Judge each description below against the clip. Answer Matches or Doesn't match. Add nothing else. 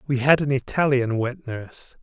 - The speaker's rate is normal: Matches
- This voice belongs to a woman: Doesn't match